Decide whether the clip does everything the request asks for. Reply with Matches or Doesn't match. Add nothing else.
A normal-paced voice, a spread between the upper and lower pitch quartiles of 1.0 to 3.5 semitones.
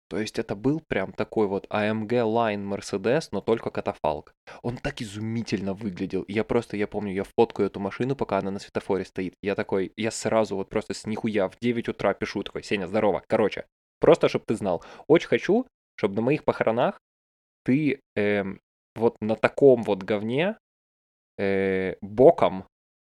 Doesn't match